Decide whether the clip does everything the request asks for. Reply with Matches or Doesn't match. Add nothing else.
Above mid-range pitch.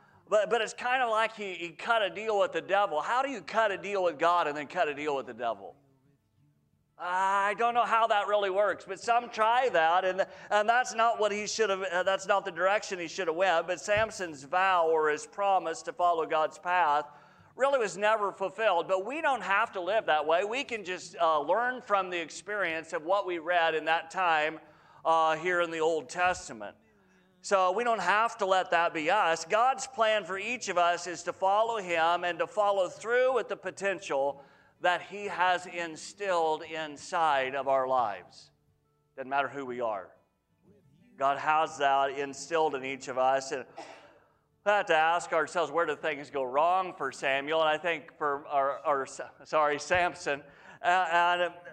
Doesn't match